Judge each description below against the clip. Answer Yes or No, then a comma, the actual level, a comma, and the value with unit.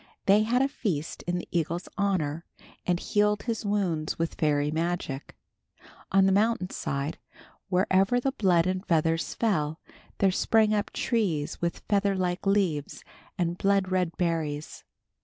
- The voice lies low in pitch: No, medium, 185 Hz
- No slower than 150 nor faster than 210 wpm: No, average, 140 wpm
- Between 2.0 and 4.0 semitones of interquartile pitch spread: Yes, average, 3.7 semitones